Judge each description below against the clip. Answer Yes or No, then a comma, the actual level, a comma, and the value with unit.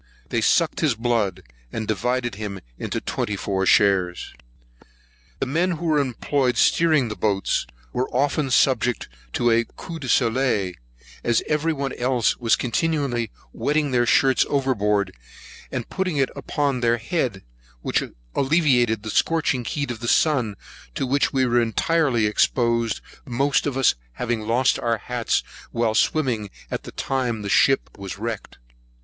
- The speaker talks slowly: No, average, 150 wpm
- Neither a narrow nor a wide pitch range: Yes, average, 3.8 semitones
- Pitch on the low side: Yes, low, 125 Hz